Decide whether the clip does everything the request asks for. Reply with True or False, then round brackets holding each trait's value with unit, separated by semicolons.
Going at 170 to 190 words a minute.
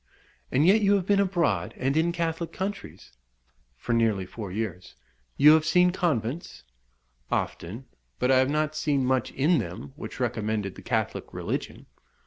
False (155 wpm)